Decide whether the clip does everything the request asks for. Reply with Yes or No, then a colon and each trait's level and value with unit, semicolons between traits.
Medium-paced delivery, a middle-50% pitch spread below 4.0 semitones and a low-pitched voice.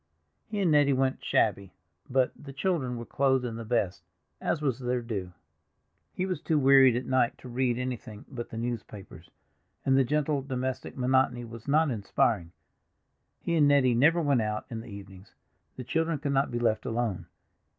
Yes: average, 180 wpm; average, 3.3 semitones; low, 125 Hz